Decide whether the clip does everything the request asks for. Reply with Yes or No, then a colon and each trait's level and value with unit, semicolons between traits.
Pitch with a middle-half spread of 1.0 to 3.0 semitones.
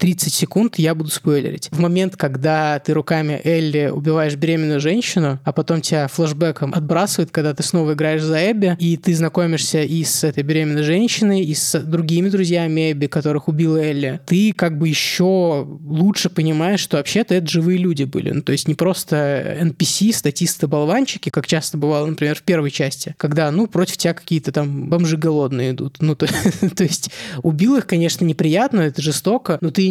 Yes: narrow, 2.6 semitones